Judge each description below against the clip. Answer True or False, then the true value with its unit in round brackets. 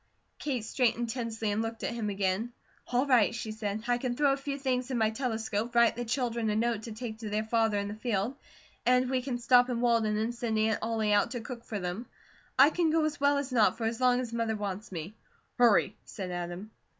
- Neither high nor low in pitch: False (230 Hz)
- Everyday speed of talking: False (235 wpm)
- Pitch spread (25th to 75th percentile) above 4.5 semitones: False (2.5 semitones)